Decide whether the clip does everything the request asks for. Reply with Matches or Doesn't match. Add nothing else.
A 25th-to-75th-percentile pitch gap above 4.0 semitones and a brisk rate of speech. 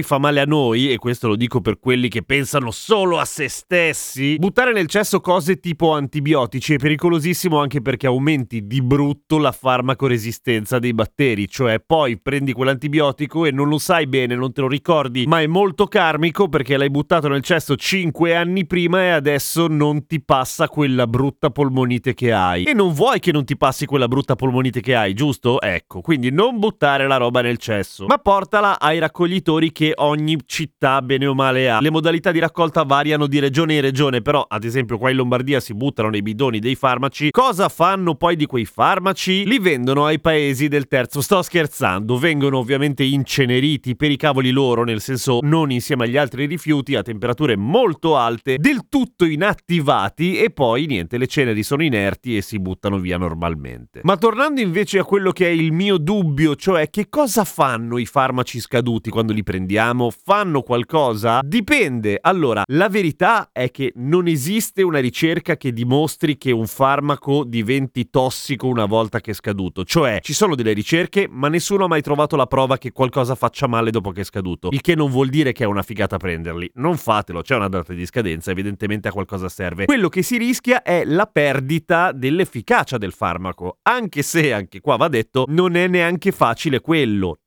Matches